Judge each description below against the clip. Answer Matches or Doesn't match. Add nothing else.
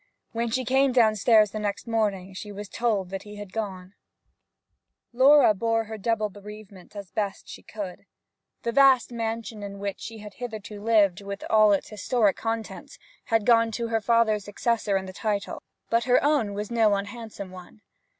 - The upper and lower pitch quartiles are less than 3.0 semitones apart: Matches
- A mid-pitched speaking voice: Doesn't match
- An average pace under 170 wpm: Doesn't match